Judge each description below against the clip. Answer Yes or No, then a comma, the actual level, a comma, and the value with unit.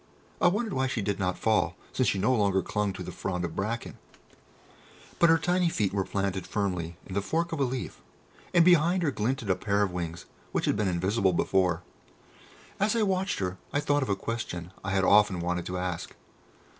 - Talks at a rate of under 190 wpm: No, fast, 205 wpm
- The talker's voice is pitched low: Yes, low, 100 Hz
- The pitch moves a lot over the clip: Yes, wide, 7.6 semitones